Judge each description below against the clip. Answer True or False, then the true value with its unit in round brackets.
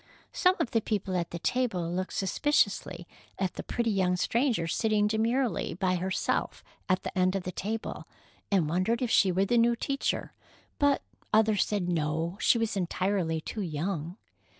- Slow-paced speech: False (170 wpm)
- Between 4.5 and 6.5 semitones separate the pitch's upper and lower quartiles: False (4.0 semitones)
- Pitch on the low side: False (195 Hz)